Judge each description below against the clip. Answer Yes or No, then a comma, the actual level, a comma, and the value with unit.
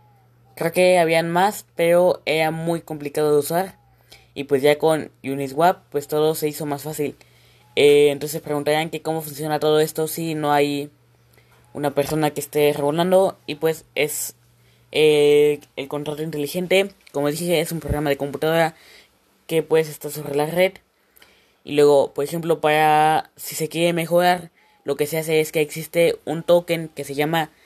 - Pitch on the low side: No, medium, 155 Hz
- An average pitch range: No, narrow, 2.1 semitones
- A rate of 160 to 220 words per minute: Yes, average, 170 wpm